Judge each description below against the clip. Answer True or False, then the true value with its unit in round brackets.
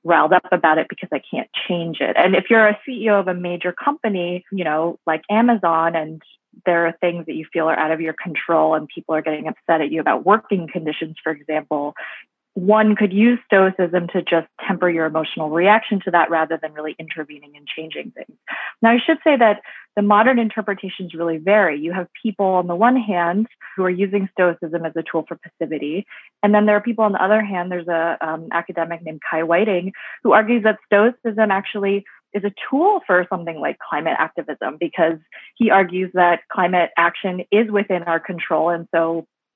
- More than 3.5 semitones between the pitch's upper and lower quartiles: True (4.2 semitones)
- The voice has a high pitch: False (180 Hz)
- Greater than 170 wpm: True (200 wpm)